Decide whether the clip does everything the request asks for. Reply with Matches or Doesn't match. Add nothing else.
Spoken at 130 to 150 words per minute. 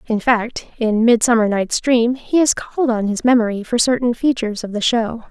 Doesn't match